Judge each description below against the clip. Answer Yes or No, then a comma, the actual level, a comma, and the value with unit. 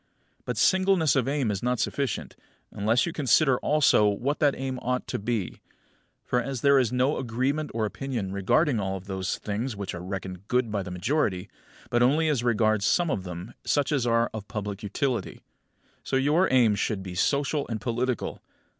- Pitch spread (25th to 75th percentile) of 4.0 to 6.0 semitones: Yes, average, 5.2 semitones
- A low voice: Yes, low, 120 Hz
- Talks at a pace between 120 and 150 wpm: No, average, 180 wpm